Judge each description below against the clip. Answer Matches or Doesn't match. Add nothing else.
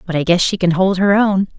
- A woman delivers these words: Matches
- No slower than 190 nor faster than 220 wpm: Doesn't match